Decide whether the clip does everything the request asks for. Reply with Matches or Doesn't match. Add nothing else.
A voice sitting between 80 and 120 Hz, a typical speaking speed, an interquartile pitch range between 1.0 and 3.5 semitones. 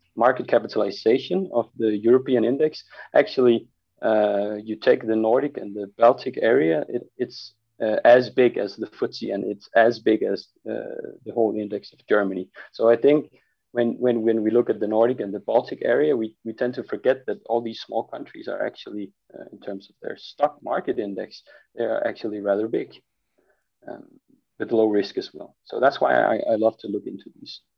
Matches